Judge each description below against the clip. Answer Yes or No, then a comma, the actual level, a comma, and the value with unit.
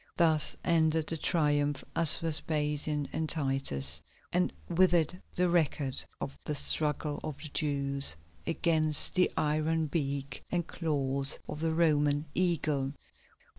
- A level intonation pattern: Yes, narrow, 2.3 semitones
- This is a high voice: No, medium, 150 Hz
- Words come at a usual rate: No, slow, 130 wpm